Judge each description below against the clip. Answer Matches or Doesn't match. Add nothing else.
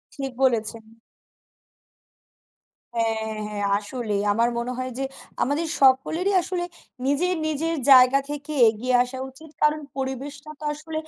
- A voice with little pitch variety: Doesn't match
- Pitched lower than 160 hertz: Doesn't match